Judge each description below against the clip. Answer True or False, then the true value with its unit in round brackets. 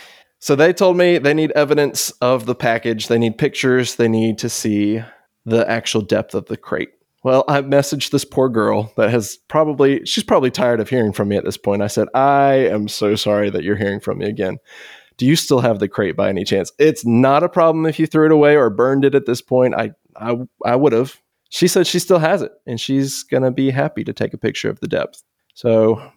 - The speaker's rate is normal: False (235 wpm)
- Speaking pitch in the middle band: False (130 Hz)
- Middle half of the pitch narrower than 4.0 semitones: False (4.5 semitones)